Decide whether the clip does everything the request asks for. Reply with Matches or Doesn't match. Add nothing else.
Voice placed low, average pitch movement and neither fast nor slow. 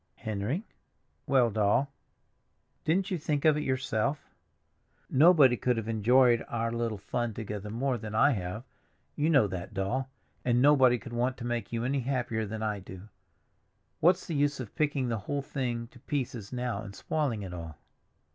Matches